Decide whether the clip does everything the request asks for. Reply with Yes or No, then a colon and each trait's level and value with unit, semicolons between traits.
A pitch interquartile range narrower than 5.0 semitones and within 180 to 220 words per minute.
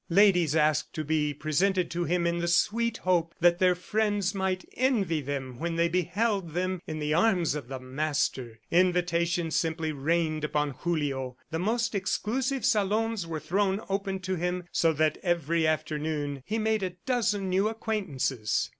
No: average, 4.1 semitones; average, 165 wpm